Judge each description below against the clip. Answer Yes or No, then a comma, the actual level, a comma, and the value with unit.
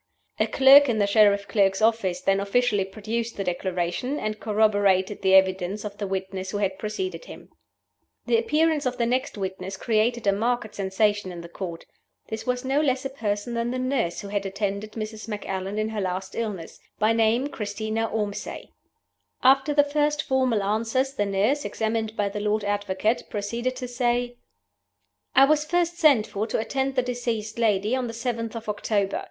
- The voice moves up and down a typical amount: Yes, average, 3.7 semitones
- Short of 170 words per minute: No, average, 180 wpm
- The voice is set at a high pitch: Yes, high, 220 Hz